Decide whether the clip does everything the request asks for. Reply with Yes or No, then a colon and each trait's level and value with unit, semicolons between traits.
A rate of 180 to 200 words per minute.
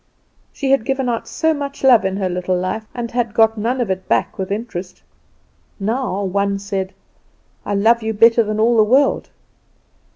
Yes: average, 185 wpm